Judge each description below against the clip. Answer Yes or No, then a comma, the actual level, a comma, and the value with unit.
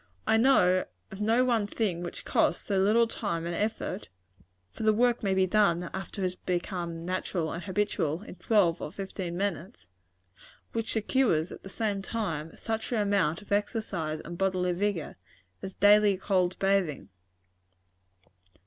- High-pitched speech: Yes, high, 195 Hz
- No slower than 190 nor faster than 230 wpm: No, average, 160 wpm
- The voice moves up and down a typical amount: Yes, average, 3.5 semitones